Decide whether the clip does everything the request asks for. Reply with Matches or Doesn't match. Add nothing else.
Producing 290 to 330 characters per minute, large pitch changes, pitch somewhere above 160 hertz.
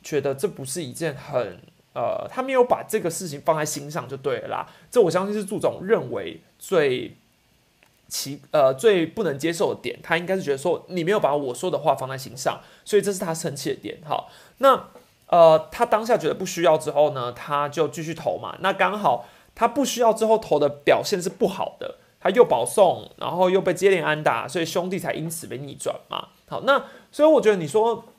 Matches